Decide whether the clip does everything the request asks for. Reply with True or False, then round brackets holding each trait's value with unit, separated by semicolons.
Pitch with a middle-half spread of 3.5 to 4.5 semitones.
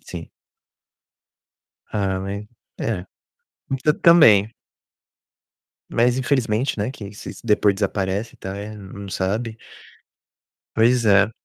False (2.9 semitones)